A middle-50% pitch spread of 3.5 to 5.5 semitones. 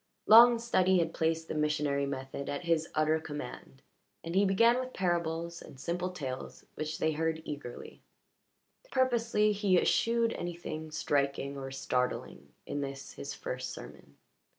Yes: average, 4.8 semitones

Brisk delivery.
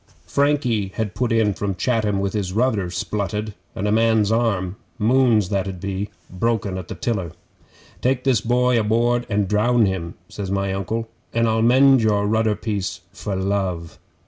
No: average, 170 wpm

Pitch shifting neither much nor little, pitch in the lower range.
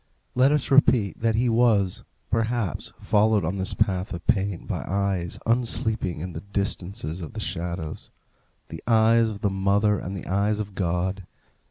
Yes: average, 3.4 semitones; low, 100 Hz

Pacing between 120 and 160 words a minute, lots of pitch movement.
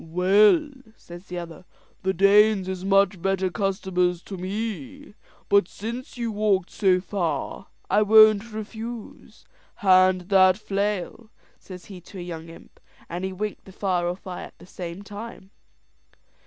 No: average, 150 wpm; narrow, 2.6 semitones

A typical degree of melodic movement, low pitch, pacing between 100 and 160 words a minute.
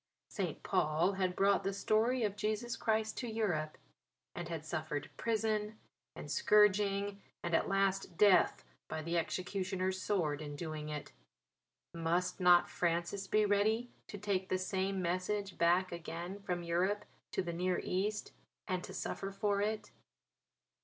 No: average, 3.2 semitones; high, 190 Hz; average, 145 wpm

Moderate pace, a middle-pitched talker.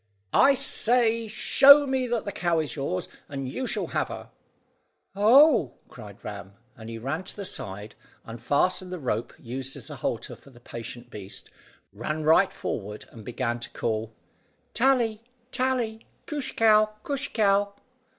Yes: average, 155 wpm; medium, 165 Hz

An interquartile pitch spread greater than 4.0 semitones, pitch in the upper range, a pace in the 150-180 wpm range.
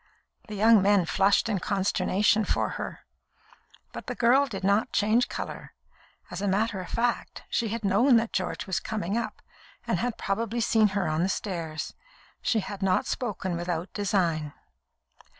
No: average, 3.2 semitones; high, 200 Hz; average, 165 wpm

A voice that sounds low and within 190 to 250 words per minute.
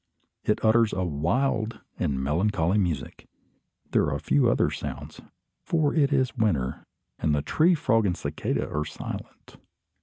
No: low, 105 Hz; average, 145 wpm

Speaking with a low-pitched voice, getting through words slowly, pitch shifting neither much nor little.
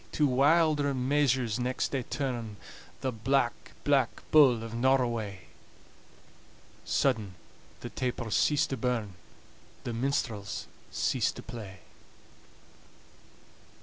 Yes: low, 125 Hz; slow, 100 wpm; average, 3.3 semitones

